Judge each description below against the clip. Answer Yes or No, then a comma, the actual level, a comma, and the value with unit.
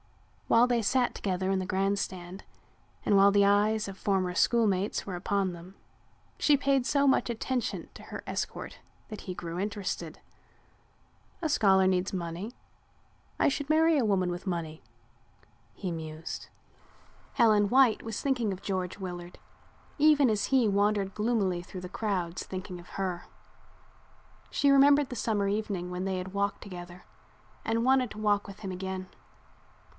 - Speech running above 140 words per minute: Yes, average, 155 wpm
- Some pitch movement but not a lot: Yes, average, 3.7 semitones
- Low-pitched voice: No, high, 200 Hz